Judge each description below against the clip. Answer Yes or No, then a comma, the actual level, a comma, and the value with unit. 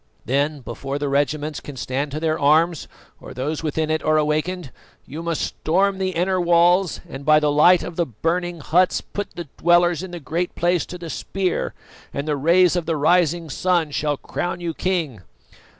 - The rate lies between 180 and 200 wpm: Yes, average, 190 wpm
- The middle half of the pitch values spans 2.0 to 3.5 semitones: Yes, average, 3.0 semitones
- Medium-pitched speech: Yes, medium, 165 Hz